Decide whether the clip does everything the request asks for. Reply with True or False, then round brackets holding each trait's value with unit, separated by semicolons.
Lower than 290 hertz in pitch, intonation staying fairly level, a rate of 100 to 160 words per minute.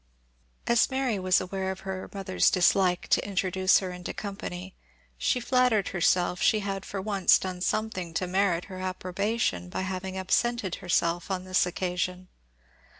True (185 Hz; 1.7 semitones; 150 wpm)